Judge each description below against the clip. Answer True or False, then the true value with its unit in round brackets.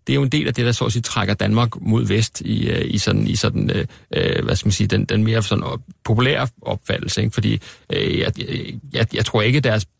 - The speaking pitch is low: True (110 Hz)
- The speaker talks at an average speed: False (250 wpm)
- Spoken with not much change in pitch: True (2.1 semitones)